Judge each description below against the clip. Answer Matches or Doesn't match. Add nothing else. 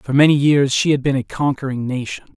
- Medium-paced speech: Doesn't match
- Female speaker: Doesn't match